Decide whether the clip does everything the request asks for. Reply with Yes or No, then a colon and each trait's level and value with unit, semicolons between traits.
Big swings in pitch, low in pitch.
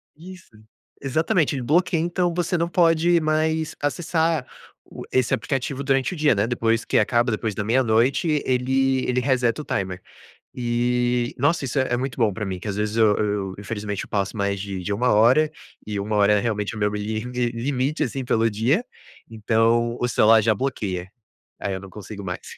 No: average, 4.8 semitones; low, 120 Hz